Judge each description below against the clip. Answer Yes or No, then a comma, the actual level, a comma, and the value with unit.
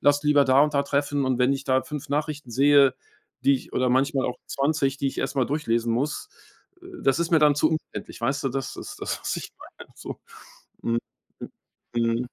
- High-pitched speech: No, medium, 140 Hz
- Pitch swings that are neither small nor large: No, narrow, 2.0 semitones